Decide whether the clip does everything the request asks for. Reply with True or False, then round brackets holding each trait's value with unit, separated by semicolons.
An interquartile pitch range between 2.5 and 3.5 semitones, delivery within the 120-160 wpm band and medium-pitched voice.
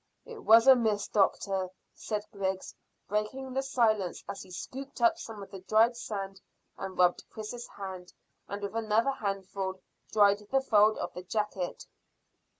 False (3.1 semitones; 155 wpm; 210 Hz)